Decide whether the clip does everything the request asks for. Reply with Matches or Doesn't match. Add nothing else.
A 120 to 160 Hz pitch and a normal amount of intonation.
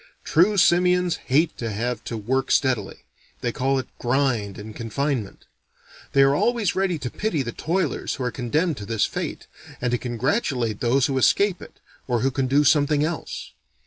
Matches